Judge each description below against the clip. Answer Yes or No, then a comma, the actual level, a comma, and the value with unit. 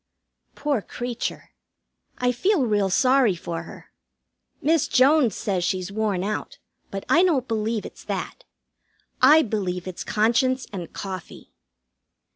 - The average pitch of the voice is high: Yes, high, 220 Hz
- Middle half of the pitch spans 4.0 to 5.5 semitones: Yes, average, 5.2 semitones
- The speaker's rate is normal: No, slow, 125 wpm